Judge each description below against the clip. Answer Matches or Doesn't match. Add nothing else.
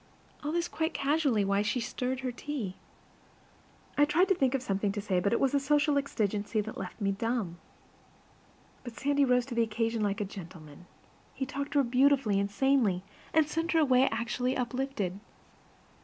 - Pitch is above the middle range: Matches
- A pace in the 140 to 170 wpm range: Doesn't match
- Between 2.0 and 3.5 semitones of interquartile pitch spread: Doesn't match